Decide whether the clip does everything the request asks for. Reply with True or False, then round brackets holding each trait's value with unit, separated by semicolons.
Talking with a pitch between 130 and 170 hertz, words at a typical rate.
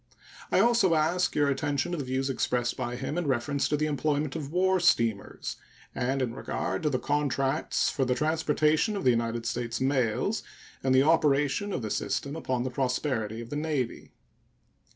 True (140 Hz; 180 wpm)